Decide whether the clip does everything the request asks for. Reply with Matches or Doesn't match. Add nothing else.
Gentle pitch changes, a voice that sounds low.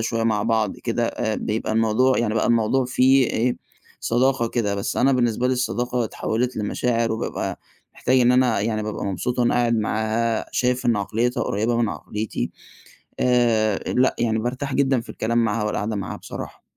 Matches